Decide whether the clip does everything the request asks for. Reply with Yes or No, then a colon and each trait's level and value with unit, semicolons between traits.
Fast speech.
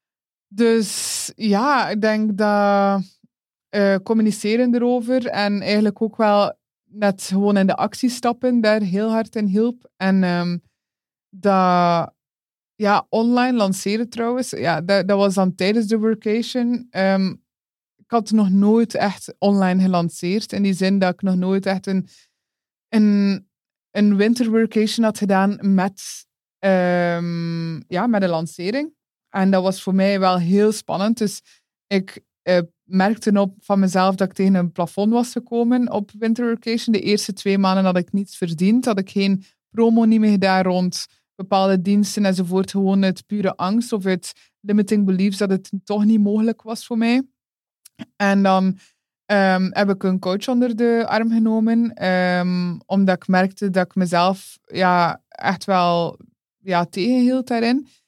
No: average, 155 wpm